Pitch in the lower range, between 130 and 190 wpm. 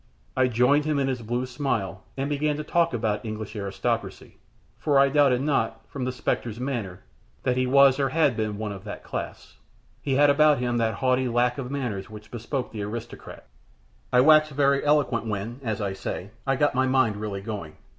No: low, 125 Hz; average, 200 wpm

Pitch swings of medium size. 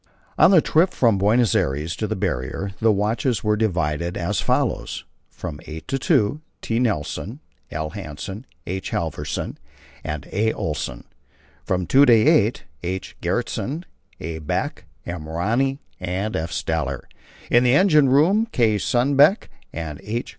No: wide, 6.9 semitones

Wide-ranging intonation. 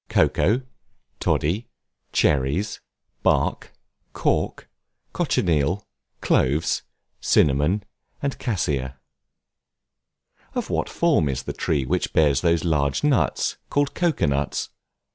Yes: wide, 6.8 semitones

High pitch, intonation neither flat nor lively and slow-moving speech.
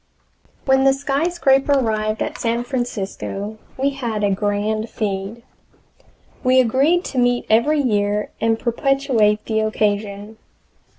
Yes: high, 230 Hz; average, 4.1 semitones; slow, 120 wpm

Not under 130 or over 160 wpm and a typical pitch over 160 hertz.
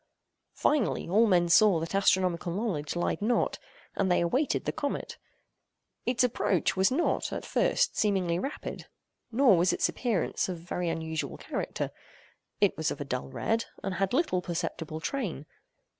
Yes: average, 155 wpm; high, 190 Hz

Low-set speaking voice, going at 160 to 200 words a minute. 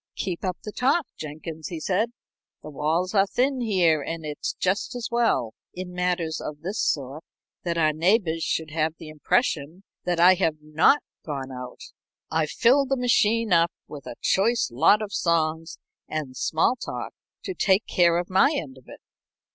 No: medium, 170 Hz; average, 175 wpm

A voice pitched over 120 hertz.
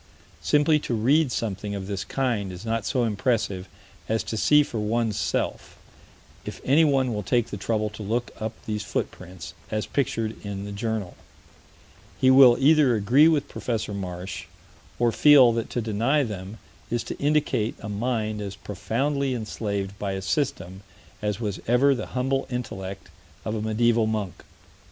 No: low, 110 Hz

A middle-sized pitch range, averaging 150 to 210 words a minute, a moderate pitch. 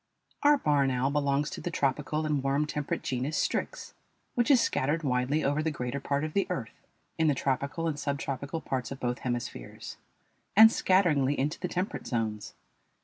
Yes: average, 3.2 semitones; average, 175 wpm; medium, 145 Hz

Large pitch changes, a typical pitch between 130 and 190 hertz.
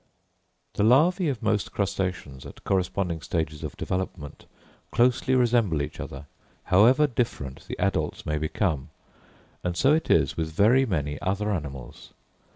No: wide, 7.5 semitones; very low, 95 Hz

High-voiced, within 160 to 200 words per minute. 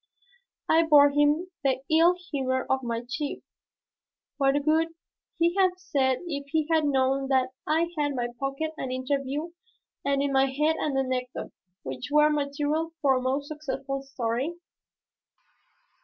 No: very high, 280 Hz; average, 150 wpm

